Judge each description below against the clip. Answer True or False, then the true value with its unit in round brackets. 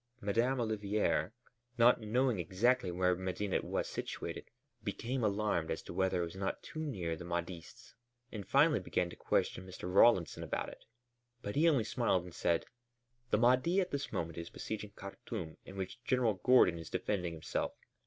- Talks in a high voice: False (100 Hz)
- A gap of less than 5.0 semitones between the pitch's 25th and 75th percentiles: False (5.3 semitones)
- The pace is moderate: True (170 wpm)